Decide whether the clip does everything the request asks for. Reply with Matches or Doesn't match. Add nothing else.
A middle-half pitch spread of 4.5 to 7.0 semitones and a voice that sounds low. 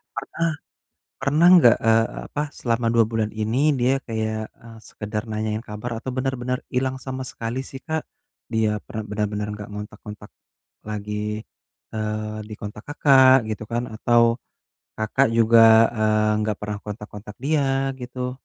Doesn't match